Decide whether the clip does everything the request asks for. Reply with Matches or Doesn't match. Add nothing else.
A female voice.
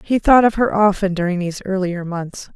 Matches